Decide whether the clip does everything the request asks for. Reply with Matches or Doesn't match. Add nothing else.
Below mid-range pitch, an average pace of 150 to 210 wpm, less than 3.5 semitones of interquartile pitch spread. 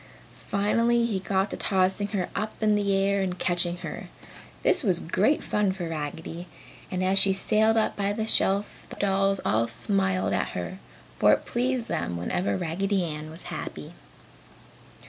Doesn't match